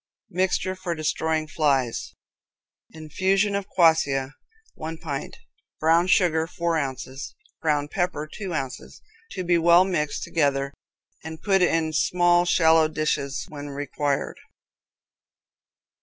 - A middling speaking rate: No, slow, 110 wpm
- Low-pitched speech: No, medium, 160 Hz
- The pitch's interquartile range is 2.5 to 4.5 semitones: Yes, average, 3.3 semitones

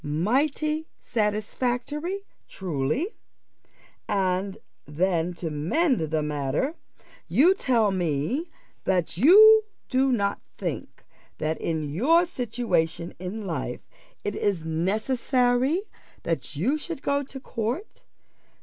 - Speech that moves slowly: Yes, slow, 105 wpm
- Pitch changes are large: Yes, wide, 8.9 semitones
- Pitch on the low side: No, high, 215 Hz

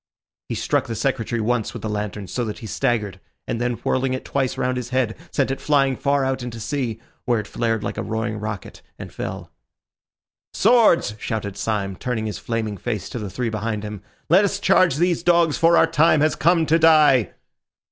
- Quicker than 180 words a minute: Yes, average, 200 wpm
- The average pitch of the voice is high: No, low, 120 Hz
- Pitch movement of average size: Yes, average, 5.0 semitones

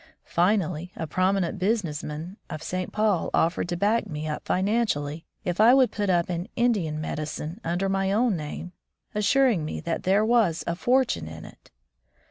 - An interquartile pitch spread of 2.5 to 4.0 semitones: No, average, 4.7 semitones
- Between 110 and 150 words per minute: No, average, 175 wpm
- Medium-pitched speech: Yes, medium, 180 Hz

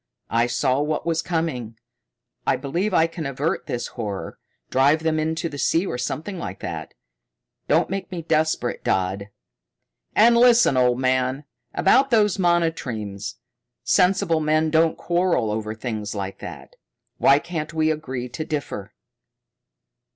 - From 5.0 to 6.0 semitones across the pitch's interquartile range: Yes, average, 5.3 semitones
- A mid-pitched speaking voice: Yes, medium, 155 Hz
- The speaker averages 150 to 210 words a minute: No, average, 140 wpm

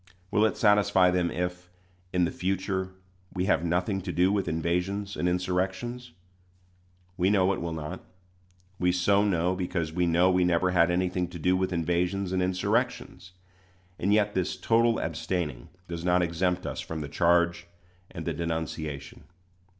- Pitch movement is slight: Yes, narrow, 1.8 semitones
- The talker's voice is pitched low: Yes, very low, 90 Hz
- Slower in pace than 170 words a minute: Yes, average, 160 wpm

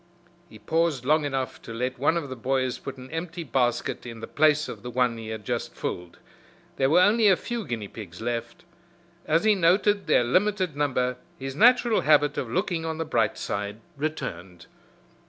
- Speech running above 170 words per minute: Yes, average, 190 wpm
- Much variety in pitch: Yes, wide, 5.9 semitones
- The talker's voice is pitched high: No, low, 135 Hz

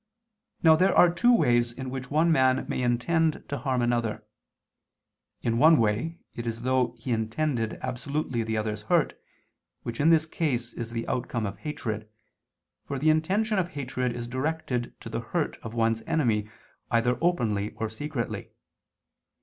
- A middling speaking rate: Yes, average, 165 wpm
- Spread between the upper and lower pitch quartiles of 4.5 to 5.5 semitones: Yes, average, 5.1 semitones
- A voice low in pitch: Yes, low, 125 Hz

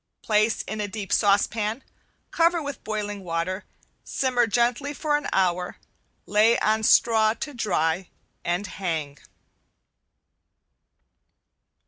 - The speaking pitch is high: Yes, high, 215 Hz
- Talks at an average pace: No, slow, 105 wpm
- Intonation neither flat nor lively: Yes, average, 4.0 semitones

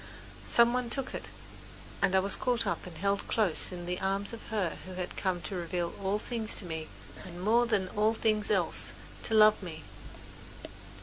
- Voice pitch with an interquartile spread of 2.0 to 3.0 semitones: No, average, 3.6 semitones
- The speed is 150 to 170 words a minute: No, average, 190 wpm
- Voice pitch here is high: Yes, high, 200 Hz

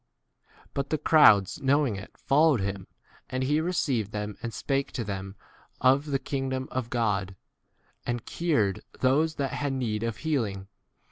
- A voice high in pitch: No, low, 130 Hz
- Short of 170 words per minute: Yes, average, 150 wpm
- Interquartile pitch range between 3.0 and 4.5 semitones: No, average, 5.2 semitones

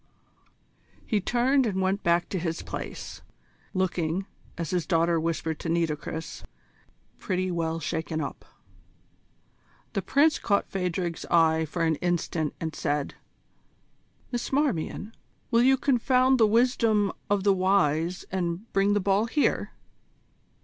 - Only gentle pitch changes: No, average, 4.5 semitones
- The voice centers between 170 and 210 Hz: Yes, medium, 185 Hz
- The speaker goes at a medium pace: No, slow, 130 wpm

